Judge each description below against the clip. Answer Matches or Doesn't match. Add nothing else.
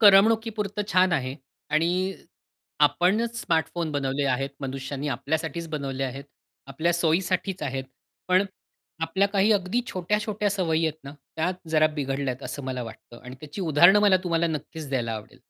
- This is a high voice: Doesn't match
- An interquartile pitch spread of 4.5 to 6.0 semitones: Matches